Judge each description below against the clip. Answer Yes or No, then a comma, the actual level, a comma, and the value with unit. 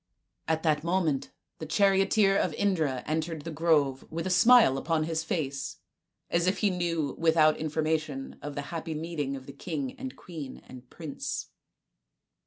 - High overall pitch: No, medium, 160 Hz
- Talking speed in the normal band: Yes, average, 155 wpm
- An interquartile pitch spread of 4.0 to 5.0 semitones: No, average, 2.9 semitones